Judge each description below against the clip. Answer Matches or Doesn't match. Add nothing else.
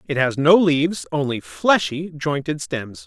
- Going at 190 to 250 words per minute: Doesn't match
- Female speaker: Doesn't match